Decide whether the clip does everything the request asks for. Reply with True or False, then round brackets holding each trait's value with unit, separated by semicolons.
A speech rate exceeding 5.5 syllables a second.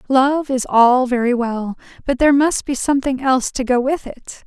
False (5.0 syllables/s)